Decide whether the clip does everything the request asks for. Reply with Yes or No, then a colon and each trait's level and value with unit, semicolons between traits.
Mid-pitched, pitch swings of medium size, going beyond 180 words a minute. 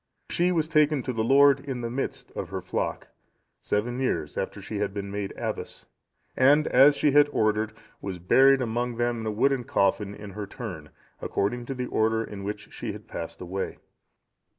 No: low, 120 Hz; average, 4.8 semitones; average, 190 wpm